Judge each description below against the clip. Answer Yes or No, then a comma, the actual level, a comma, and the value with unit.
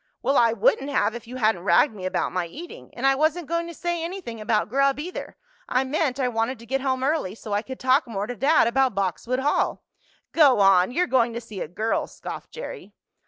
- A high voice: Yes, very high, 255 Hz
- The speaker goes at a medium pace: No, fast, 225 wpm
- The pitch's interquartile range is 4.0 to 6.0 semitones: Yes, average, 4.4 semitones